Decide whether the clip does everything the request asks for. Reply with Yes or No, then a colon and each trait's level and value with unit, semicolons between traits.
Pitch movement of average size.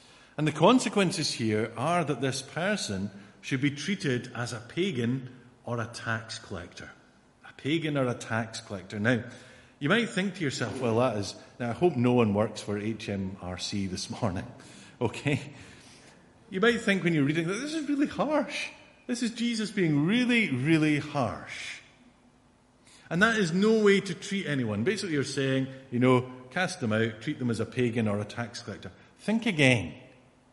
No: wide, 7.1 semitones